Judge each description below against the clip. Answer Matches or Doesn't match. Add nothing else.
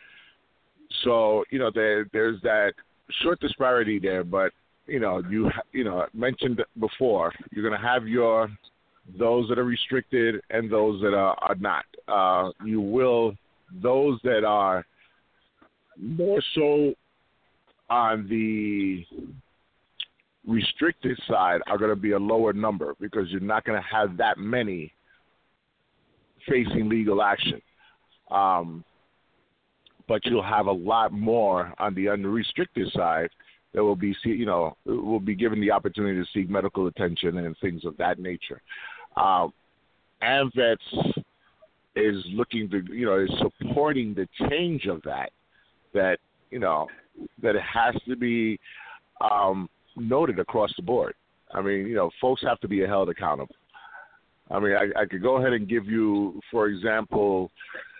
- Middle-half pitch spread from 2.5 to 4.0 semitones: Matches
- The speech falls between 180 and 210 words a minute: Doesn't match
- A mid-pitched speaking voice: Doesn't match